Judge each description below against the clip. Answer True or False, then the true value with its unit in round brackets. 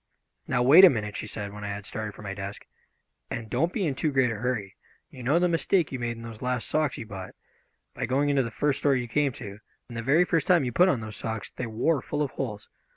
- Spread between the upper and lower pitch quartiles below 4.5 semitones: False (5.0 semitones)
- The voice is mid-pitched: False (125 Hz)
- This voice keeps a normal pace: False (265 wpm)